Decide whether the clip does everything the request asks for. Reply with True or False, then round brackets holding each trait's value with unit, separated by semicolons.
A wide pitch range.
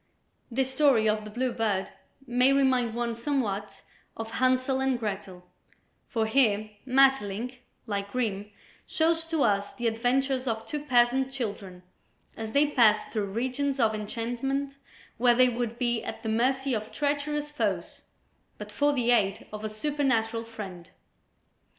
False (3.6 semitones)